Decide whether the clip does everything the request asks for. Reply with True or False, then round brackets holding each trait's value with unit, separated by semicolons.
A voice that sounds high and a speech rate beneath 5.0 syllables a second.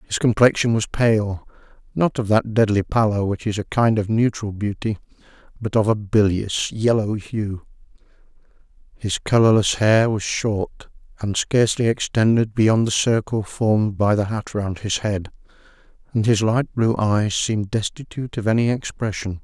False (110 Hz; 4.7 syllables/s)